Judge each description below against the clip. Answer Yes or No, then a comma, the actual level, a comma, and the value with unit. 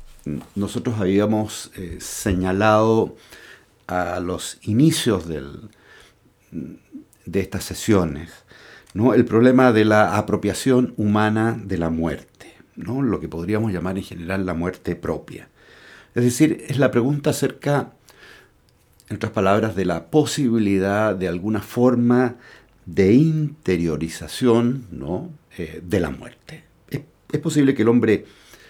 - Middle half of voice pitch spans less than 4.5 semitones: No, average, 4.8 semitones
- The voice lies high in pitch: No, low, 105 Hz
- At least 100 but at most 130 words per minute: Yes, slow, 125 wpm